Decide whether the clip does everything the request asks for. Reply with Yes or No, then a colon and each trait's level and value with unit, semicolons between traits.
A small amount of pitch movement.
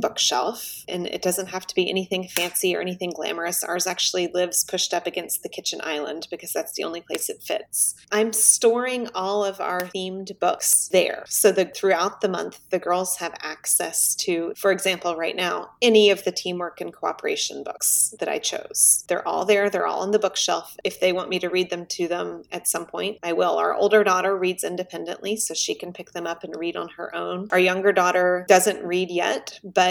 Yes: narrow, 1.9 semitones